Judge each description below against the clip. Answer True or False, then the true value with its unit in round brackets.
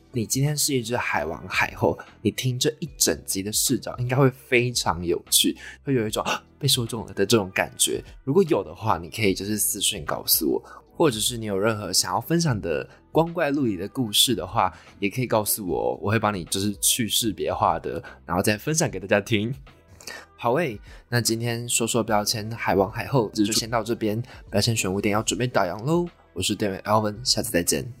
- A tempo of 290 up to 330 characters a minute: True (310 characters per minute)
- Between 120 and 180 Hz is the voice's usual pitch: False (110 Hz)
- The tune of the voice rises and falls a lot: False (3.6 semitones)